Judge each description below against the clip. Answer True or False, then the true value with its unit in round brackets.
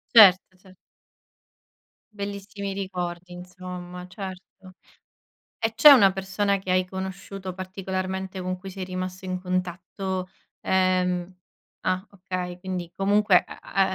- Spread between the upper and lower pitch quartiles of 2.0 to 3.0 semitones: False (1.1 semitones)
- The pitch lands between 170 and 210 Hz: True (185 Hz)